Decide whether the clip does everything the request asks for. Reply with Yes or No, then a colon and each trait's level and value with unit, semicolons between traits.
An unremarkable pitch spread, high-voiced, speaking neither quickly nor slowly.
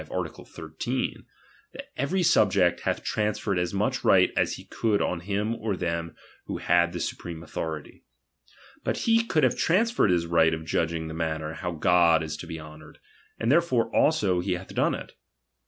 No: average, 4.8 semitones; very low, 90 Hz; average, 180 wpm